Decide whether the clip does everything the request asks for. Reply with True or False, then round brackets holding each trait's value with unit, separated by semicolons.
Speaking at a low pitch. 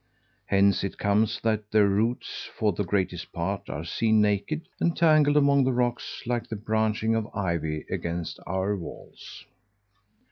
True (105 Hz)